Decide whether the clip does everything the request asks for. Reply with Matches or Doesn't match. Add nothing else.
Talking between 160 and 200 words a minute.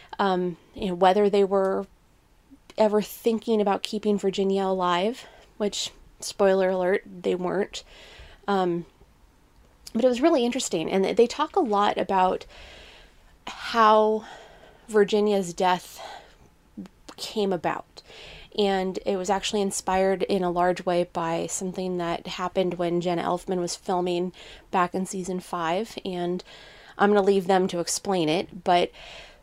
Doesn't match